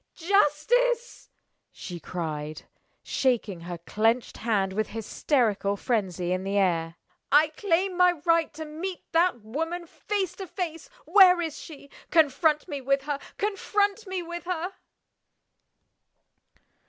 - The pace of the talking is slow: Yes, slow, 125 wpm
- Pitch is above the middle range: Yes, very high, 300 Hz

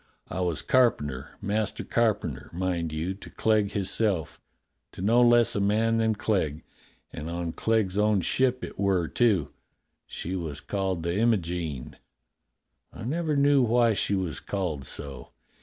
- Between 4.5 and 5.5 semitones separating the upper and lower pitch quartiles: Yes, average, 4.9 semitones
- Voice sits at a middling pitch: No, low, 100 Hz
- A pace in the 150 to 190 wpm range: Yes, average, 155 wpm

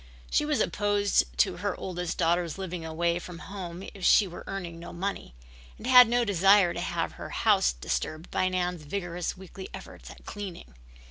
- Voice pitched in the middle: Yes, medium, 180 Hz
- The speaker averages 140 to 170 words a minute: No, average, 180 wpm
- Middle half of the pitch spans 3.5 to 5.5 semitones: No, average, 2.8 semitones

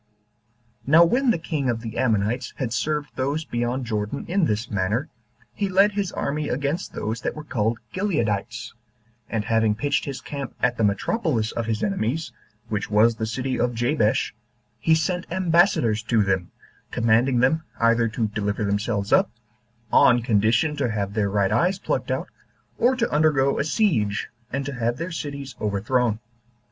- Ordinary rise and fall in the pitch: No, wide, 5.8 semitones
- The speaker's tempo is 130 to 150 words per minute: No, average, 165 wpm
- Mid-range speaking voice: No, low, 120 Hz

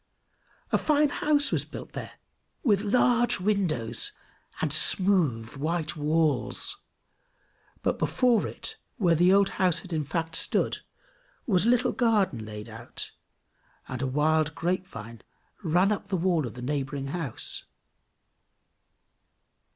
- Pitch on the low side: No, medium, 165 Hz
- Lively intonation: Yes, wide, 6.2 semitones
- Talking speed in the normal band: No, slow, 130 wpm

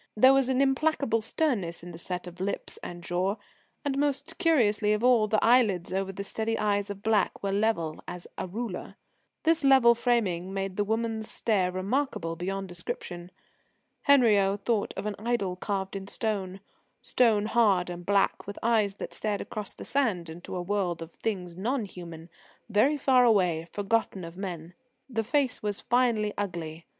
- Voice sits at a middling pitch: No, high, 205 Hz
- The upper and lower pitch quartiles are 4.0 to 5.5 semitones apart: Yes, average, 4.4 semitones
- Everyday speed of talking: Yes, average, 170 wpm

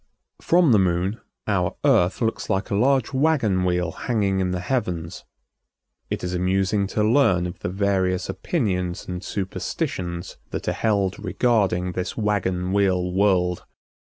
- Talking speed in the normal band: Yes, average, 145 wpm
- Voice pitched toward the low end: Yes, very low, 95 Hz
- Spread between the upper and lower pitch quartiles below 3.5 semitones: Yes, average, 2.8 semitones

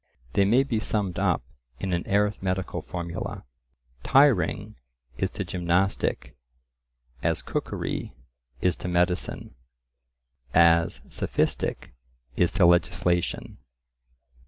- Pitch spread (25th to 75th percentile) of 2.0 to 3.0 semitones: Yes, narrow, 2.5 semitones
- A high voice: No, very low, 90 Hz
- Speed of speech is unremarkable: No, slow, 60 wpm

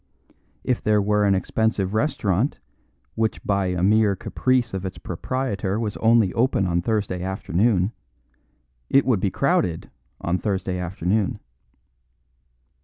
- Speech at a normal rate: No, slow, 125 wpm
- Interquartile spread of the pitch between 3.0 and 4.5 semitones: Yes, average, 3.3 semitones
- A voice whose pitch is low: Yes, low, 100 Hz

